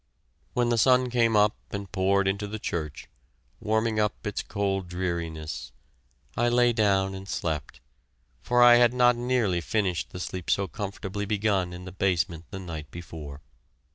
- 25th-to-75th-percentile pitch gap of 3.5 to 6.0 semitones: Yes, average, 3.9 semitones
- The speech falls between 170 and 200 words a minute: No, average, 160 wpm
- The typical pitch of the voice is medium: No, low, 100 Hz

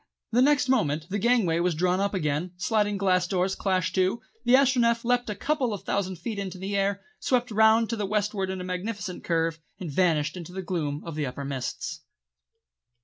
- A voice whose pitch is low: No, high, 190 Hz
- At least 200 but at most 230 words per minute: Yes, fast, 205 wpm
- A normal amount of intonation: Yes, average, 4.1 semitones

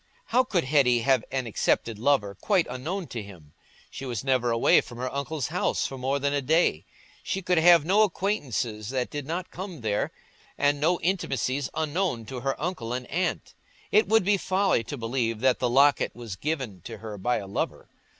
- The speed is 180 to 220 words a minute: Yes, average, 195 wpm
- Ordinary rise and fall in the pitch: No, wide, 6.2 semitones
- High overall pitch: No, low, 135 Hz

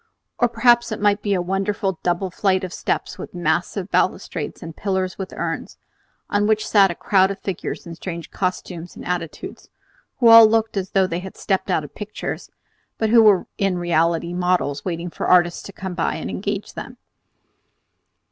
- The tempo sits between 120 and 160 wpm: No, average, 185 wpm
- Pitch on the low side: No, high, 190 Hz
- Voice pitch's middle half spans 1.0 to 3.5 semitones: Yes, average, 2.8 semitones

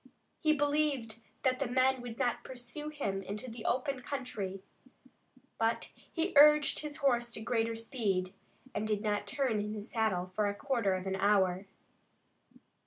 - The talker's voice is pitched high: Yes, high, 230 Hz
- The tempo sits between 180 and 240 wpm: No, average, 160 wpm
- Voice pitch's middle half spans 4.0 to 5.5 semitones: Yes, average, 4.6 semitones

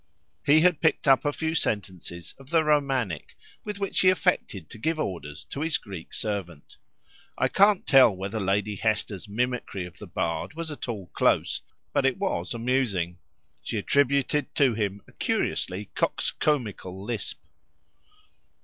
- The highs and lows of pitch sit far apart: Yes, wide, 7.2 semitones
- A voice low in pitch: Yes, low, 120 Hz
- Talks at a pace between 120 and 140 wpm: No, average, 150 wpm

